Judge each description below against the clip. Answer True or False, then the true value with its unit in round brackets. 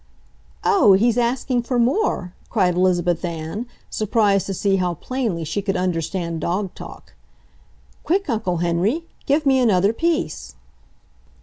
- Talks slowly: True (130 wpm)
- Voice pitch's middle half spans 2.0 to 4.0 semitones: False (5.6 semitones)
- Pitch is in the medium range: False (195 Hz)